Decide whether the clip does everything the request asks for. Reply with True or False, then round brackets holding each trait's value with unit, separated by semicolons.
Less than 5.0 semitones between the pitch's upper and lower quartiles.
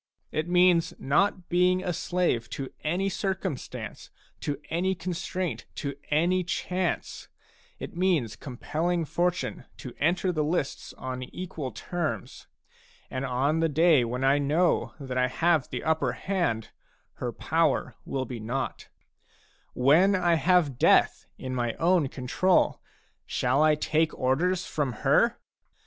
False (5.3 semitones)